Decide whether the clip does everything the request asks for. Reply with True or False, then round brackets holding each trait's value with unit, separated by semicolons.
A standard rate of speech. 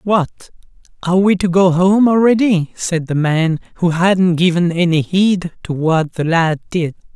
True (170 wpm)